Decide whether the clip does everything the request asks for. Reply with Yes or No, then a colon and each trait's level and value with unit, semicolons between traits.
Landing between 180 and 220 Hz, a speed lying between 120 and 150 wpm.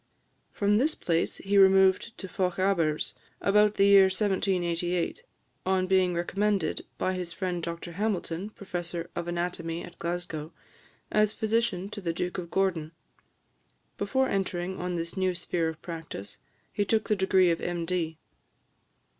Yes: medium, 185 Hz; average, 140 wpm